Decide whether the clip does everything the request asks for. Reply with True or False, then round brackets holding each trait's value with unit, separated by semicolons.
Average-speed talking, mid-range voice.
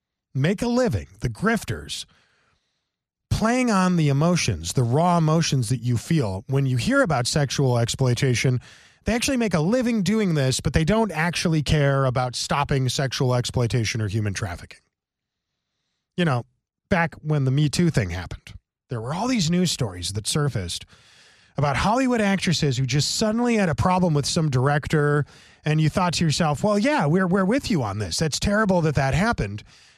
True (175 wpm; 145 Hz)